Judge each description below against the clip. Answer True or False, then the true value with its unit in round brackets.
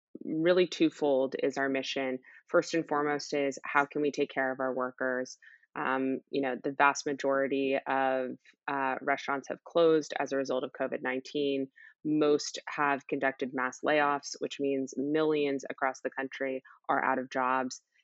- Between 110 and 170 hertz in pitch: True (135 Hz)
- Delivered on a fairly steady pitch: True (1.7 semitones)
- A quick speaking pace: False (160 wpm)